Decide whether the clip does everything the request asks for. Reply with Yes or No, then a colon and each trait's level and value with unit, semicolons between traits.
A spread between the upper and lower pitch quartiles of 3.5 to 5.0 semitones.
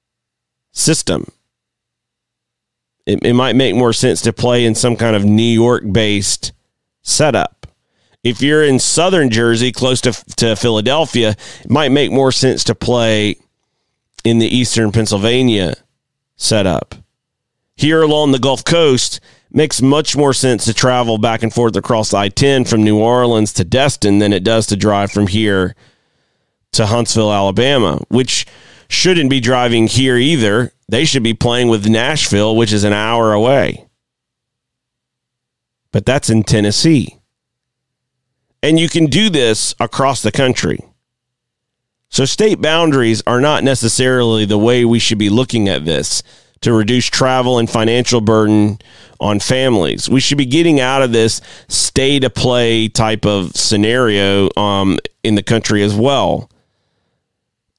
No: average, 3.1 semitones